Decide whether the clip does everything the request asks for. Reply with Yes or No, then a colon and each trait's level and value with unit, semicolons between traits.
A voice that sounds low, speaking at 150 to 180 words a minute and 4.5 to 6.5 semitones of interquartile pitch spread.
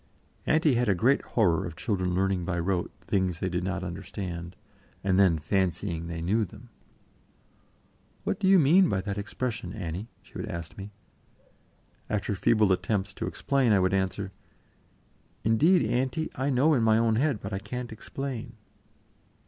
Yes: low, 100 Hz; average, 165 wpm; average, 4.8 semitones